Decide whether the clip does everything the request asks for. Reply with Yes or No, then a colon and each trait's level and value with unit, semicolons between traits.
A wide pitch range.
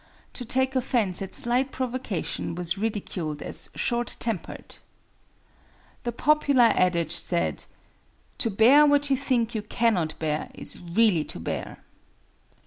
Yes: wide, 6.4 semitones